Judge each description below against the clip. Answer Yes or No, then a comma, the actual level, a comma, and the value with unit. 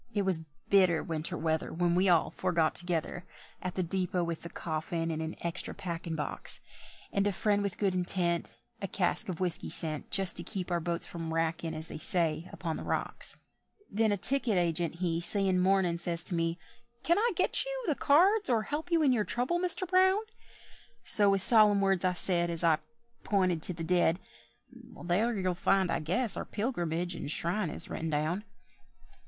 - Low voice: No, medium, 180 Hz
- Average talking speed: Yes, average, 190 wpm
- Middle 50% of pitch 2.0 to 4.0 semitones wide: Yes, average, 3.3 semitones